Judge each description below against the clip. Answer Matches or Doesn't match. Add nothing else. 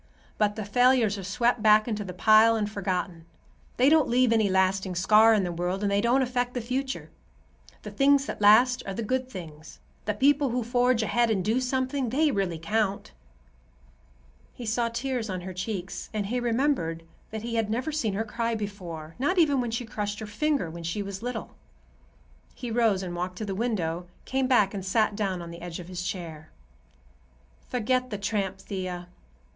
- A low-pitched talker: Doesn't match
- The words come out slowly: Doesn't match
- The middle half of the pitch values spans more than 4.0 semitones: Matches